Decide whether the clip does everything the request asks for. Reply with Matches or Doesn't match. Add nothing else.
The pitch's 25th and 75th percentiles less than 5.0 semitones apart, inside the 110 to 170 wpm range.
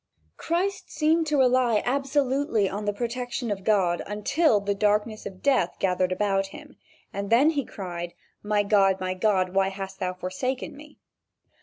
Doesn't match